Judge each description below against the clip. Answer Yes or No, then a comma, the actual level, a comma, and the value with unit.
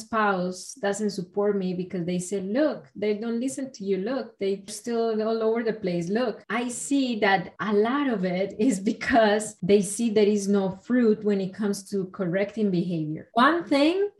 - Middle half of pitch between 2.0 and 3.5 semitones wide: Yes, average, 3.1 semitones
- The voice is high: Yes, high, 210 Hz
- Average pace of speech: Yes, average, 185 wpm